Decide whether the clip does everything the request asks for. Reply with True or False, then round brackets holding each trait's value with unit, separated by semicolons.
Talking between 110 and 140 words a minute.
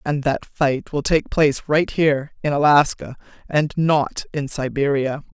True (135 wpm)